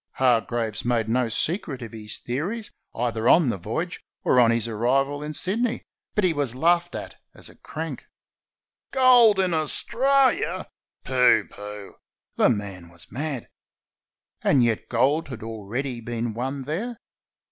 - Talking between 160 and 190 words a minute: No, average, 145 wpm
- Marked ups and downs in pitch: Yes, wide, 6.9 semitones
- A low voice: Yes, low, 130 Hz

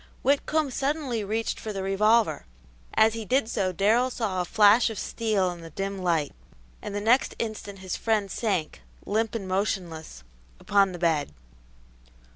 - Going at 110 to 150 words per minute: No, average, 160 wpm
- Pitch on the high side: Yes, high, 205 Hz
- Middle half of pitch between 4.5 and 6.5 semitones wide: No, average, 3.4 semitones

